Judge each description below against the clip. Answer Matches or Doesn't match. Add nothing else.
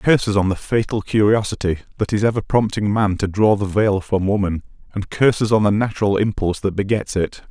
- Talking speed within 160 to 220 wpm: Matches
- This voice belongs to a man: Matches